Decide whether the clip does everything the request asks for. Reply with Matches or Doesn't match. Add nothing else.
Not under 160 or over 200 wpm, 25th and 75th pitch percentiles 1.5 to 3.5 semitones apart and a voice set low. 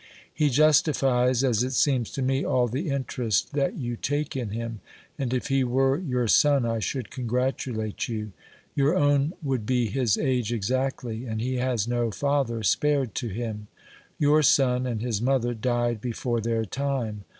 Matches